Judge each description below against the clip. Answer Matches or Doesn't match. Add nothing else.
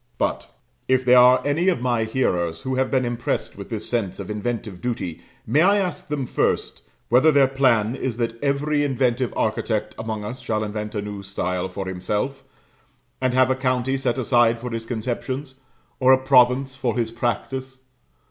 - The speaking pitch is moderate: Doesn't match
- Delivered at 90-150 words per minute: Doesn't match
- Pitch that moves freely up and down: Doesn't match